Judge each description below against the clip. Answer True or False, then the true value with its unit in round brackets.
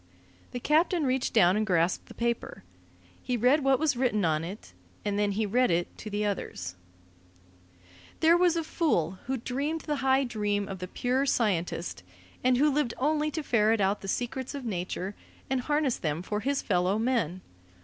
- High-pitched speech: True (235 Hz)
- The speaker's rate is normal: True (180 wpm)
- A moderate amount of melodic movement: False (5.8 semitones)